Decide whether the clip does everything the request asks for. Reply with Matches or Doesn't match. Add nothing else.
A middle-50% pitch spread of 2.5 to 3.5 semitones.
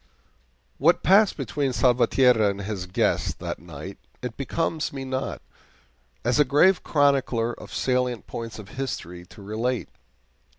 Doesn't match